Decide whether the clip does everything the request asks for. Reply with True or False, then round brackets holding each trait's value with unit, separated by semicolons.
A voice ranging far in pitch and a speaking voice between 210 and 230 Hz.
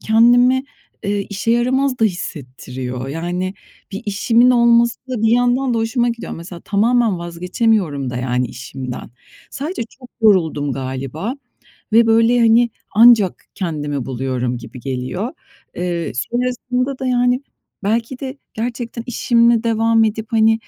True (7.0 semitones; 220 Hz)